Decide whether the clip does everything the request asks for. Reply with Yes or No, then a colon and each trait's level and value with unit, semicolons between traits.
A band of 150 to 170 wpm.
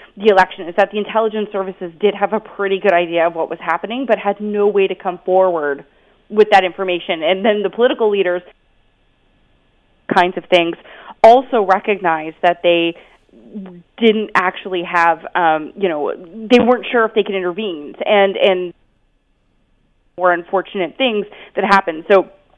Yes: average, 160 wpm